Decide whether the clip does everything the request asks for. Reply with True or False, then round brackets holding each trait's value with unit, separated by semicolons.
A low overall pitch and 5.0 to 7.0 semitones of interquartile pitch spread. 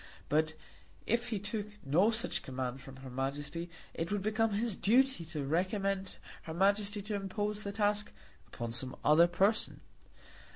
False (195 Hz; 5.6 semitones)